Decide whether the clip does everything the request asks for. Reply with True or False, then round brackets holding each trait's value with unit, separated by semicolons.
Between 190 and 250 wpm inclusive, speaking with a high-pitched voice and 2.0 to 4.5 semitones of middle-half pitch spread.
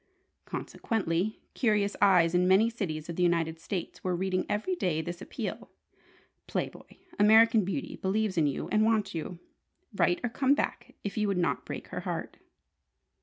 False (170 wpm; 195 Hz; 4.0 semitones)